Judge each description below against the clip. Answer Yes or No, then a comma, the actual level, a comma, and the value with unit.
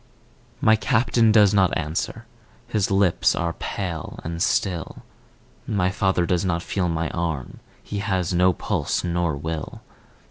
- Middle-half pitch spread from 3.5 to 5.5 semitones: No, average, 3.1 semitones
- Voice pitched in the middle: No, very low, 90 Hz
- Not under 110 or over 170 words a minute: Yes, average, 140 wpm